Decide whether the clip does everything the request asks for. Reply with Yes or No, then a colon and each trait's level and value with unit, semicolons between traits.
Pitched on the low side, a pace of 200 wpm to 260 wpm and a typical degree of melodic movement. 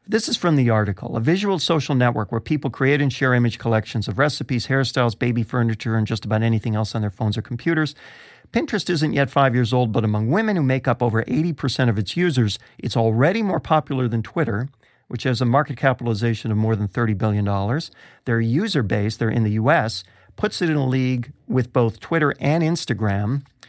Yes: low, 125 Hz; fast, 205 wpm; average, 4.4 semitones